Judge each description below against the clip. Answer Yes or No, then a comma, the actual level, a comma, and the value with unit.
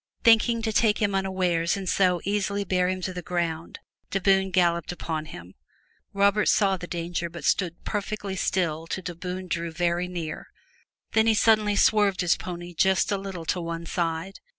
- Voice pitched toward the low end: No, medium, 185 Hz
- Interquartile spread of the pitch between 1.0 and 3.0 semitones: Yes, narrow, 2.6 semitones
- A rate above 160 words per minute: Yes, average, 180 wpm